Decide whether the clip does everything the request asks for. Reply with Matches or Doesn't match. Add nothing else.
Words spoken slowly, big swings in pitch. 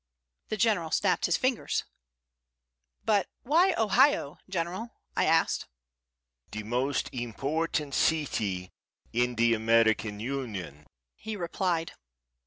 Matches